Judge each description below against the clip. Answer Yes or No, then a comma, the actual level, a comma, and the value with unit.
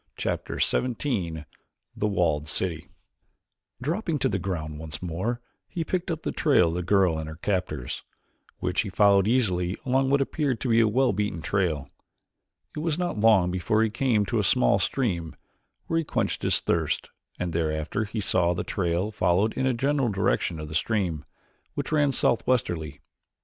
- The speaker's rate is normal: Yes, average, 175 wpm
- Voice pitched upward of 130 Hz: No, low, 100 Hz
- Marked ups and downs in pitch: Yes, wide, 6.9 semitones